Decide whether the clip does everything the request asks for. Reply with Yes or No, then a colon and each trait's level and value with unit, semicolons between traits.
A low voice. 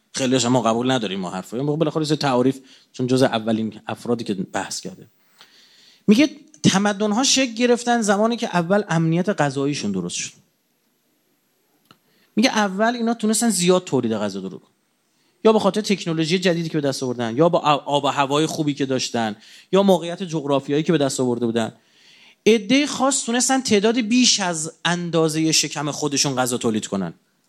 No: medium, 160 Hz